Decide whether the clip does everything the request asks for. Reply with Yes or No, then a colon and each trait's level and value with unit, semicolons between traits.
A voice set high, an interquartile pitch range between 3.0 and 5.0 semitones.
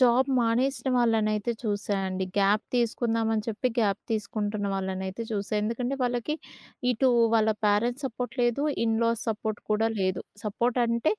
No: high, 225 Hz; narrow, 2.6 semitones